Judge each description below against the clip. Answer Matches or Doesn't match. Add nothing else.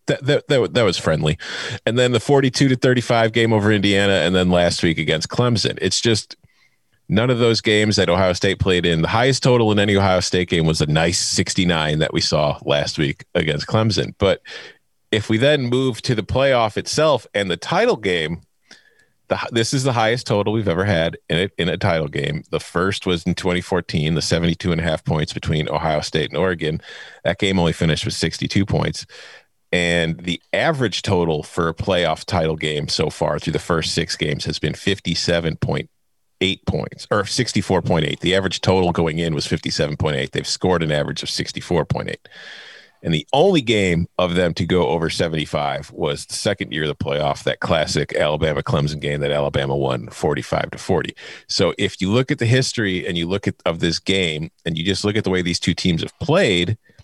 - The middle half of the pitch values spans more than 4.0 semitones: Matches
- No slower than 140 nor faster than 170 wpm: Doesn't match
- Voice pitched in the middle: Doesn't match